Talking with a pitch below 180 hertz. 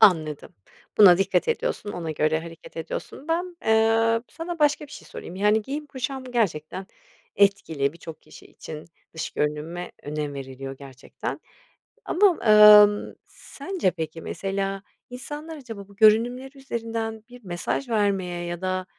No: high, 205 Hz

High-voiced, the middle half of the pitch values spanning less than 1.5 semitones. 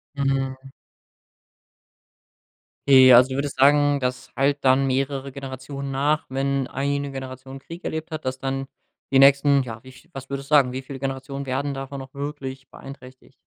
No: low, 135 Hz; narrow, 1.1 semitones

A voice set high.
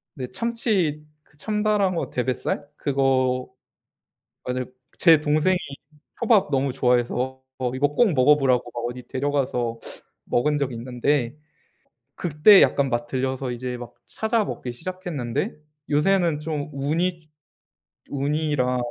No: medium, 140 Hz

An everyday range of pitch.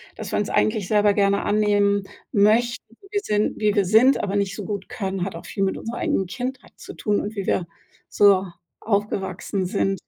No: narrow, 1.6 semitones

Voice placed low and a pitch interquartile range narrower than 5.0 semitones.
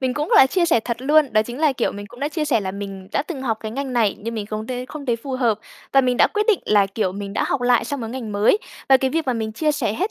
No: high, 245 Hz; average, 4.5 semitones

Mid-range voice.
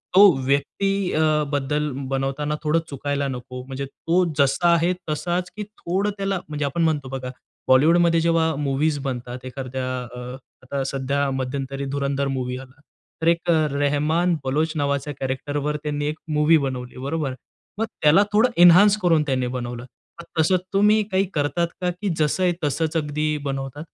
Yes: medium, 145 Hz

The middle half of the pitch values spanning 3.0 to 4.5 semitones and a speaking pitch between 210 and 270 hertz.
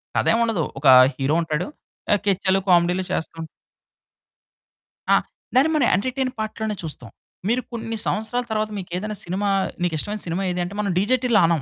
No: average, 4.1 semitones; high, 200 Hz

